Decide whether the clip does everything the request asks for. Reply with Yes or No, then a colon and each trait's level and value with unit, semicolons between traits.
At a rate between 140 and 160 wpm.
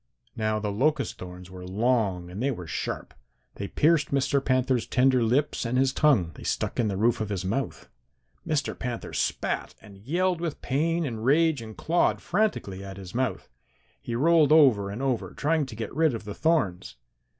No: average, 185 wpm